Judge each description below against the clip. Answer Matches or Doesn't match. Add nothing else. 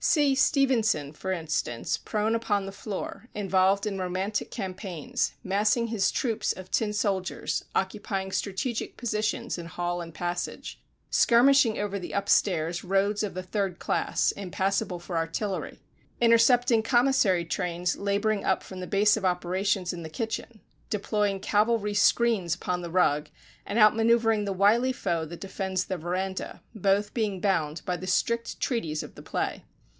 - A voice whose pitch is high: Matches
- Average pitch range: Matches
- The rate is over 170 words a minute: Doesn't match